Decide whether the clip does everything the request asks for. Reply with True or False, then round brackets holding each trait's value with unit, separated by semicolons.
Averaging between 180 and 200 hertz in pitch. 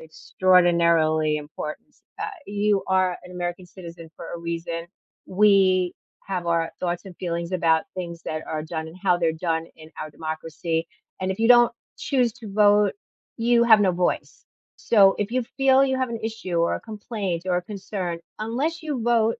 True (185 Hz)